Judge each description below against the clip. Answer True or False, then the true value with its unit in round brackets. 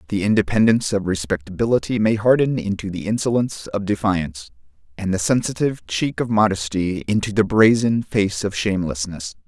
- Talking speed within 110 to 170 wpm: True (145 wpm)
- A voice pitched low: True (105 Hz)